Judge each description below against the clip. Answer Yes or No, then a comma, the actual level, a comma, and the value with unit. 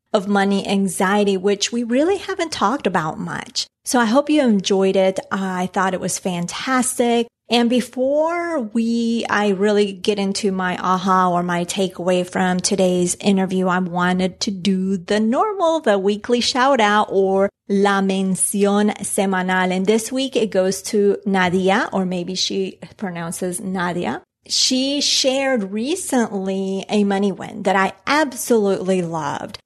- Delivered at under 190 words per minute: Yes, average, 145 wpm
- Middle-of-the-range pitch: No, high, 200 Hz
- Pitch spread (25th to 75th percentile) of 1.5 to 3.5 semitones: No, average, 3.9 semitones